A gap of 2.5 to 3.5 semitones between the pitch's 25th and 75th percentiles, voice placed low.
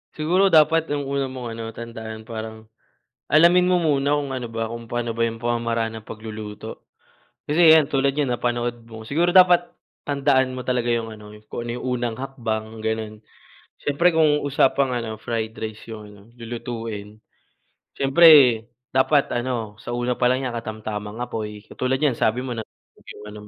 No: average, 3.9 semitones; low, 120 Hz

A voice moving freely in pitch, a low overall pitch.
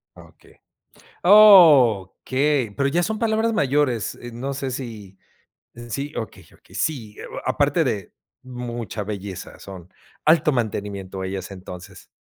Yes: wide, 6.4 semitones; low, 120 Hz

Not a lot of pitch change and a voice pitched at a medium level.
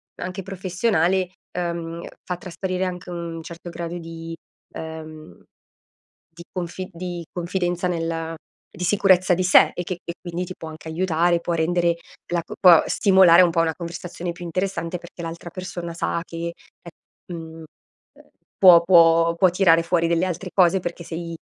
Yes: narrow, 1.4 semitones; medium, 170 Hz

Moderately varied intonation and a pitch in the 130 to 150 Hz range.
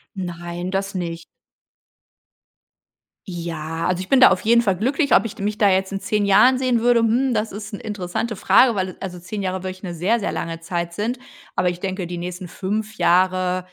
No: average, 3.4 semitones; high, 190 Hz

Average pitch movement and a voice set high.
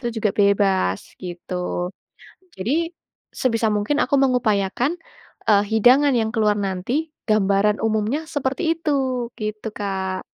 Yes: average, 4.8 semitones; high, 220 Hz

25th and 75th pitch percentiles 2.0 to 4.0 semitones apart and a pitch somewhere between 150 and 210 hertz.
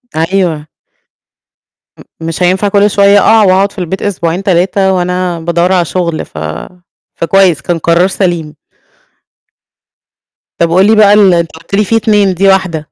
Yes: average, 2.8 semitones; medium, 185 Hz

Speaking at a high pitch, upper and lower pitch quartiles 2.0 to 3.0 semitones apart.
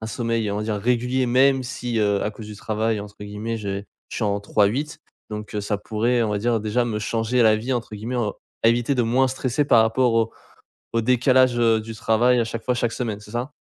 No: low, 115 Hz; narrow, 2.5 semitones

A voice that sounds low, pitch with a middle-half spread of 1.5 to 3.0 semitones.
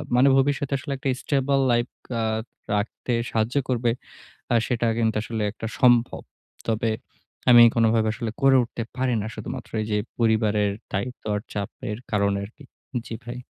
Yes: low, 115 Hz; narrow, 2.6 semitones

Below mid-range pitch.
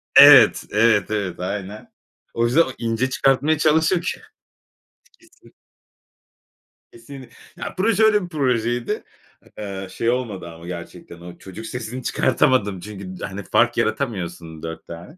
Yes: low, 115 Hz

